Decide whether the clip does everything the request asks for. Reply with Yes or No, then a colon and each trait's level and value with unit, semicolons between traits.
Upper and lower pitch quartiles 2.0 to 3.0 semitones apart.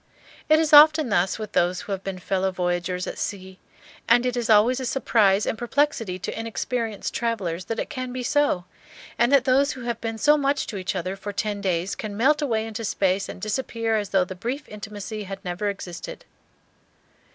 No: average, 4.6 semitones